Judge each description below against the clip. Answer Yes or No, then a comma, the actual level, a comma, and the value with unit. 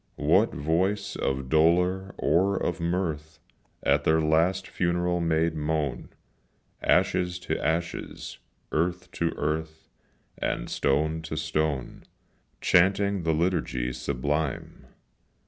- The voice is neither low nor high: No, very low, 80 Hz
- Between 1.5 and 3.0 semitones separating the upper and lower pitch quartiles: Yes, narrow, 2.5 semitones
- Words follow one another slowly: Yes, slow, 105 wpm